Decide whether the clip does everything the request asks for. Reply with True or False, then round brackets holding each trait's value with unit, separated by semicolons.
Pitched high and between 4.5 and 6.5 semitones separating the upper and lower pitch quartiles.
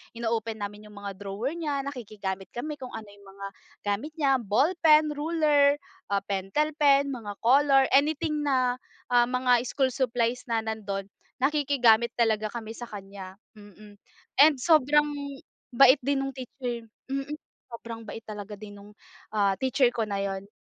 True (240 Hz; 5.1 semitones)